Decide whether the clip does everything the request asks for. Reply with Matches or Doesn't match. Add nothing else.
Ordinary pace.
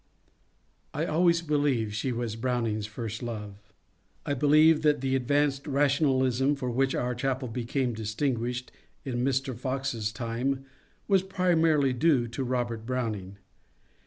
Doesn't match